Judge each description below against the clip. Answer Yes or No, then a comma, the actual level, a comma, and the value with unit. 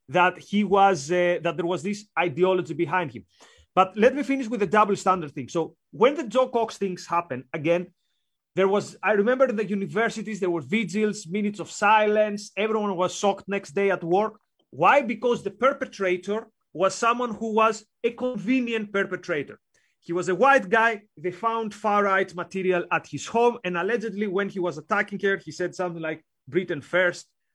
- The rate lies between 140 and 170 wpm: No, average, 185 wpm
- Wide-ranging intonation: No, average, 3.6 semitones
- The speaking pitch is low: No, high, 195 Hz